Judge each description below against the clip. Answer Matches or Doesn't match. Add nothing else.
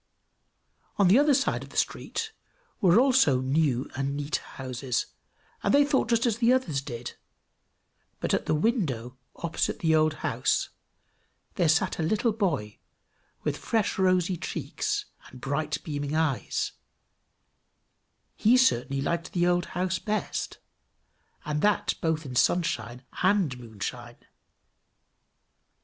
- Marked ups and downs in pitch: Matches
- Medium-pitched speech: Matches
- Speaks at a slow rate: Matches